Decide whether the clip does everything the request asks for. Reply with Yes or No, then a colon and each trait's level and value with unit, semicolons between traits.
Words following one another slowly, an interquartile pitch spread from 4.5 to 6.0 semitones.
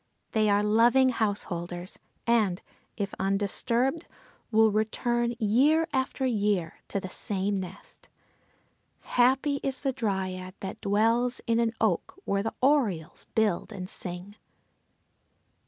No: slow, 120 wpm; average, 3.9 semitones